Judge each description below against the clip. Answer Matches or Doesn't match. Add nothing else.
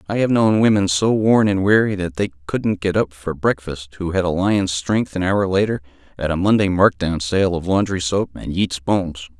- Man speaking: Matches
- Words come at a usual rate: Doesn't match